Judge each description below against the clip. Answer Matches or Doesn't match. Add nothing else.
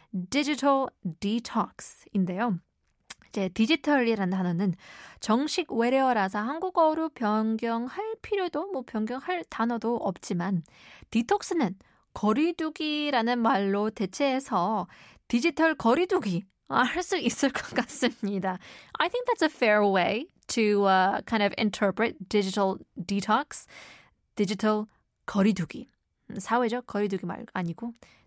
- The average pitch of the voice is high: Matches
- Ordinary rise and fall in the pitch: Doesn't match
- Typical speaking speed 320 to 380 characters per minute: Doesn't match